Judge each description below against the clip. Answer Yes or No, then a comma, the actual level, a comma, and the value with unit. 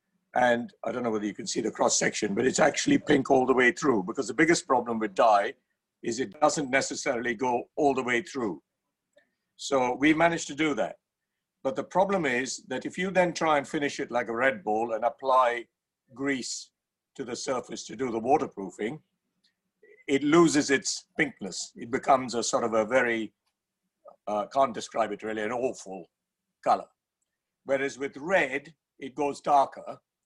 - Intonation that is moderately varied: Yes, average, 4.5 semitones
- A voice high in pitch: No, low, 135 Hz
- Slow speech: No, average, 180 wpm